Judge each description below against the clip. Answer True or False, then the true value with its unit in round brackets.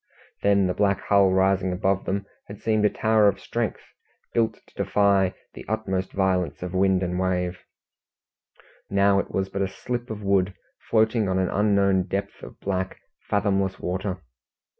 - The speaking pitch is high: False (95 Hz)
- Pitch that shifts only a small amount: True (1.5 semitones)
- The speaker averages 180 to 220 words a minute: False (160 wpm)